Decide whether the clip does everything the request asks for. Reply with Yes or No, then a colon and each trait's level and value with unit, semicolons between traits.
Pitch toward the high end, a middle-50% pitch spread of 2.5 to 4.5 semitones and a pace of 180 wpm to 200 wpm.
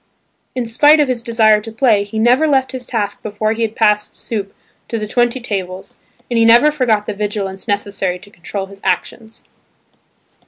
Yes: high, 220 Hz; average, 2.9 semitones; average, 185 wpm